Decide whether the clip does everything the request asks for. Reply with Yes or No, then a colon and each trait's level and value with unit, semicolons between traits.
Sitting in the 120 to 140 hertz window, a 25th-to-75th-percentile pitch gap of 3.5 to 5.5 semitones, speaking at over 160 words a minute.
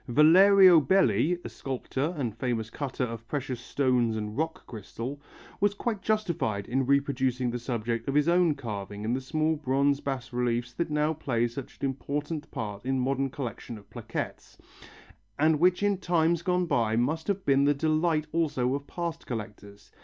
Yes: low, 135 Hz; average, 4.9 semitones; average, 170 wpm